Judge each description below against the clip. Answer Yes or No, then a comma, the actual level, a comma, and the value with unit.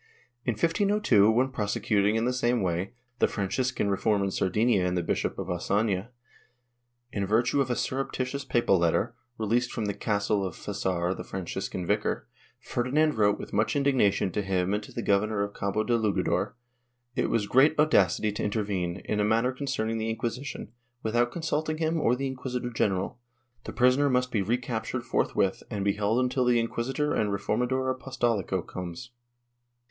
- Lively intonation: No, average, 4.1 semitones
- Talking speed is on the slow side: No, average, 170 wpm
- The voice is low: Yes, low, 110 Hz